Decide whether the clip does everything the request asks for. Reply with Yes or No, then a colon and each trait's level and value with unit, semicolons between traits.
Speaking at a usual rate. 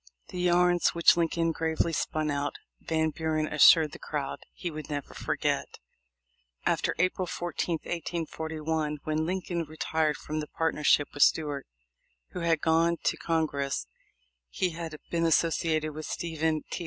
Yes: average, 145 wpm